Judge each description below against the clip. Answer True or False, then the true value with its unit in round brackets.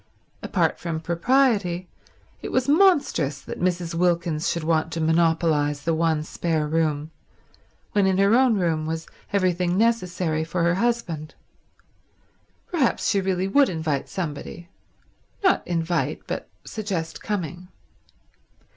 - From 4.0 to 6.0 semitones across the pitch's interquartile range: False (3.5 semitones)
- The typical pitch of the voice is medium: True (170 Hz)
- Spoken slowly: True (125 wpm)